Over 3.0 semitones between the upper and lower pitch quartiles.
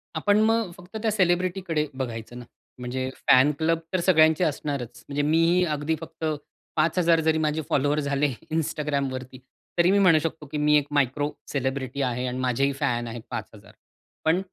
Yes: average, 4.0 semitones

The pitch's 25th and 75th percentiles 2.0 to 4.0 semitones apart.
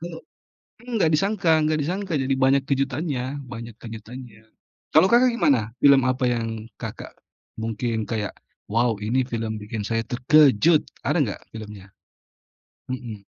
No: wide, 5.4 semitones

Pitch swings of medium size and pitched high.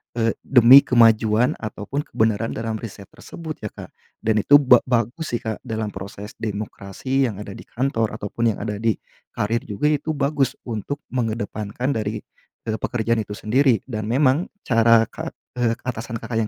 No: average, 3.0 semitones; low, 115 Hz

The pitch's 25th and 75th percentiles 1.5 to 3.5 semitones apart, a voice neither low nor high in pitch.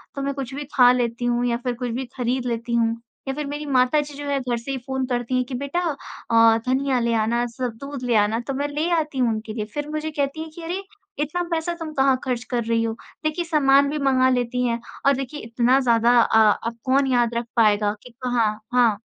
No: average, 3.1 semitones; very high, 255 Hz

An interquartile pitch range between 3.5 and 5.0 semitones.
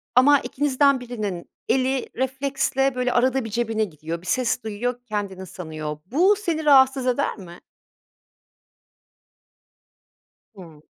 No: wide, 5.4 semitones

